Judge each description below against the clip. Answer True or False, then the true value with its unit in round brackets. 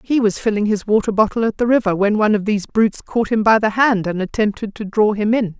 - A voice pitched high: True (215 Hz)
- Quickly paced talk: True (270 wpm)